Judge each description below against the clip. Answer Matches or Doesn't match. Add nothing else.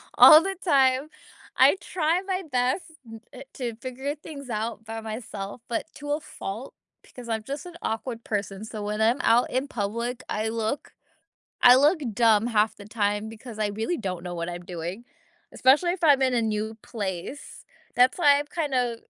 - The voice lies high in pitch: Matches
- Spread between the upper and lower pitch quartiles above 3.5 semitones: Matches